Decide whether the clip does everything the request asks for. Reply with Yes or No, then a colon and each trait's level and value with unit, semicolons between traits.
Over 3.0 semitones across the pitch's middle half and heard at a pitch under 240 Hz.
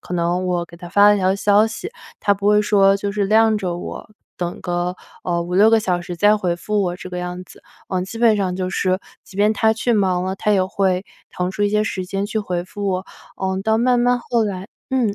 No: average, 2.7 semitones; high, 195 Hz